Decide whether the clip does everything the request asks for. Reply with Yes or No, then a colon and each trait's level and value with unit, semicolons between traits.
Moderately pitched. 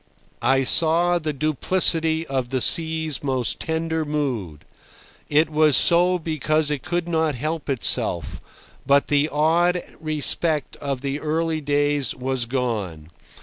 Yes: medium, 150 Hz